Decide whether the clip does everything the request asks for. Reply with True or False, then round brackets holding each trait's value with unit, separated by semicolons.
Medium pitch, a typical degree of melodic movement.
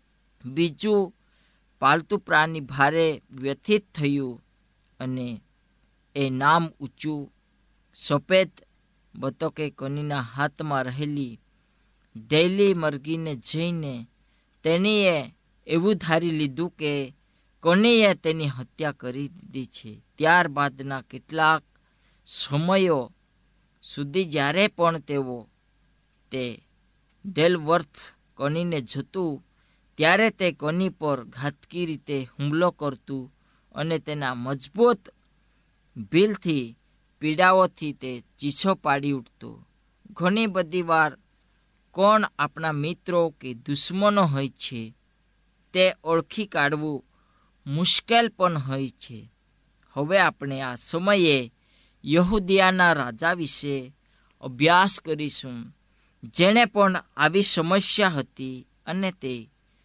True (150 Hz; 4.8 semitones)